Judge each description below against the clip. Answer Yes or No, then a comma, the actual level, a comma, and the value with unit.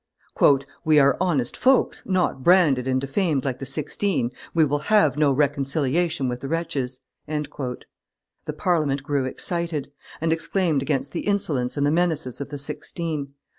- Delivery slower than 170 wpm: Yes, average, 150 wpm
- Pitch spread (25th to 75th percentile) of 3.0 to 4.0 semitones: Yes, average, 3.6 semitones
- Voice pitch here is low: No, medium, 145 Hz